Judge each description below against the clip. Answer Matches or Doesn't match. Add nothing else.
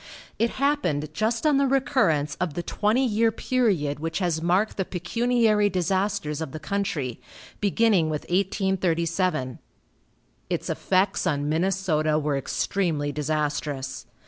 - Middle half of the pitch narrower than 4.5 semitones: Doesn't match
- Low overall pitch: Doesn't match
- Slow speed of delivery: Matches